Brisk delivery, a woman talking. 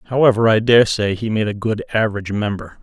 No: fast, 210 wpm; male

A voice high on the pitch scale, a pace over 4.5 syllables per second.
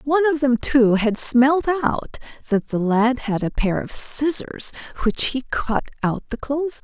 No: very high, 255 Hz; 4.3 syllables/s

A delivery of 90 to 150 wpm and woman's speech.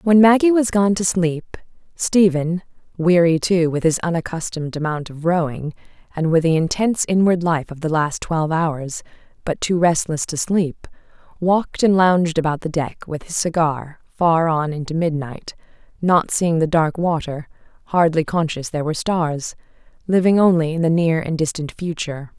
No: average, 165 wpm; female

